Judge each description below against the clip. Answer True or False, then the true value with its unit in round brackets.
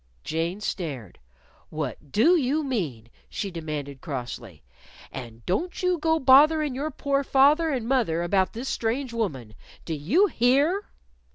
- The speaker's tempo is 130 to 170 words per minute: True (135 wpm)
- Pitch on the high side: True (225 Hz)